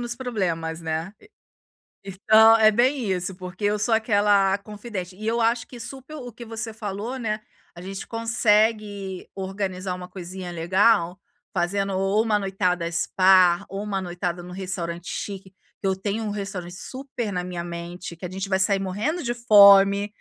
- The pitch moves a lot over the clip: No, average, 3.3 semitones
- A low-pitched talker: No, high, 195 Hz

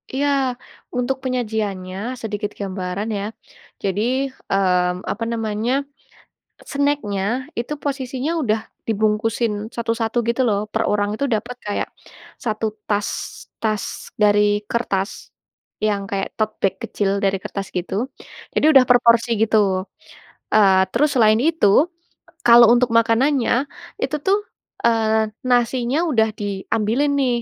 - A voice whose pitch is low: No, high, 220 Hz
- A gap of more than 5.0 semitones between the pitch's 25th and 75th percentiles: No, average, 3.2 semitones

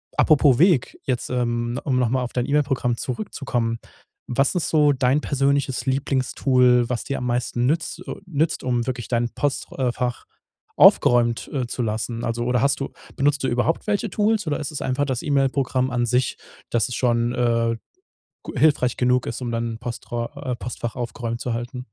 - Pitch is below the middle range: Yes, low, 125 Hz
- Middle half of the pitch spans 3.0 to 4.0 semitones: No, narrow, 2.6 semitones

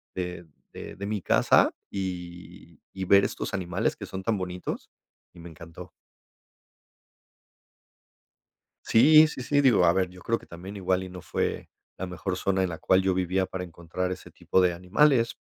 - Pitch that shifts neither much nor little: No, narrow, 1.7 semitones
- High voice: No, very low, 95 Hz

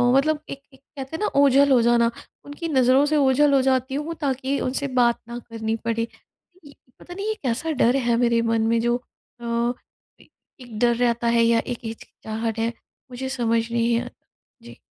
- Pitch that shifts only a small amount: No, average, 3.0 semitones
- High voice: Yes, high, 245 Hz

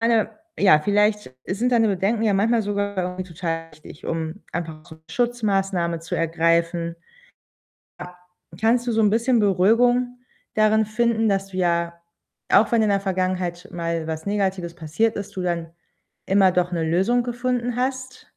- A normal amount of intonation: Yes, average, 4.7 semitones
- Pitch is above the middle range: Yes, high, 195 Hz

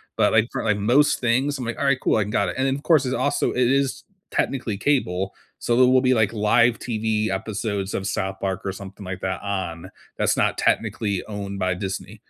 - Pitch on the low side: Yes, low, 110 Hz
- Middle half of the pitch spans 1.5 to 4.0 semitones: No, average, 4.6 semitones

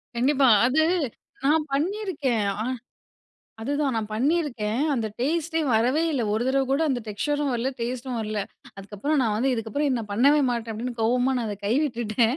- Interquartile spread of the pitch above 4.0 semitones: Yes, average, 4.4 semitones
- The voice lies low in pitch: No, very high, 250 Hz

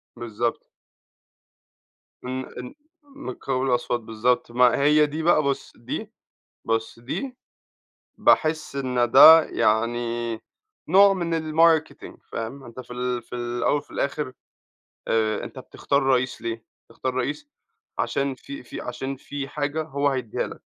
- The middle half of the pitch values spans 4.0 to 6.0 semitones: No, average, 3.6 semitones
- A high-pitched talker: No, low, 130 Hz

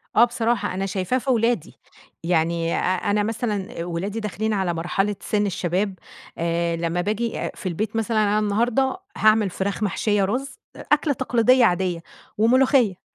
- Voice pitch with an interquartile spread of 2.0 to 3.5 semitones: No, average, 4.2 semitones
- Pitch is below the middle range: No, high, 210 Hz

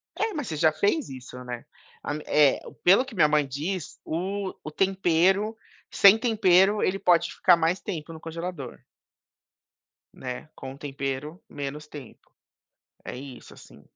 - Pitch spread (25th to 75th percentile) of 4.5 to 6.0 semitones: Yes, average, 5.1 semitones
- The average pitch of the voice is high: No, medium, 165 Hz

